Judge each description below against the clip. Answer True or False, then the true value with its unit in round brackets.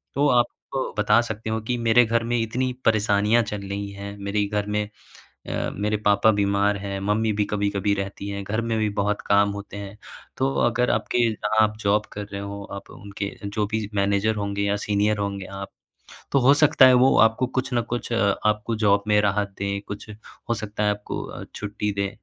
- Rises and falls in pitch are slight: True (1.7 semitones)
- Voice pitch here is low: True (105 Hz)